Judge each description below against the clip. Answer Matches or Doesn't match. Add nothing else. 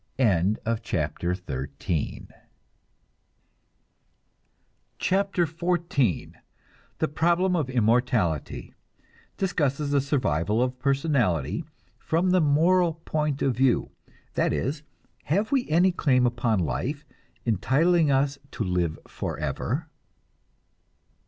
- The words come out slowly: Matches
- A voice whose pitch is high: Doesn't match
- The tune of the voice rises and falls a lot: Matches